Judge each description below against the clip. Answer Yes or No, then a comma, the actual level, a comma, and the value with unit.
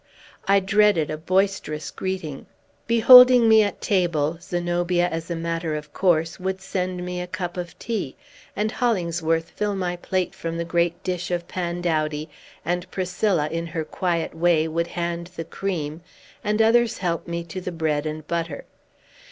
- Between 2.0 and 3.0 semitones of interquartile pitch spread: Yes, narrow, 2.5 semitones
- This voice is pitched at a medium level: Yes, medium, 175 Hz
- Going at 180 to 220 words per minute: No, average, 160 wpm